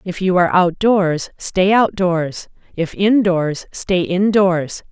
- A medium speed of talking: No, slow, 120 wpm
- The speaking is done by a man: No, female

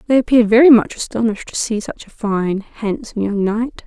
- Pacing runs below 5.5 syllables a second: No, 5.7 syllables/s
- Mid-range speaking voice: No, high, 225 Hz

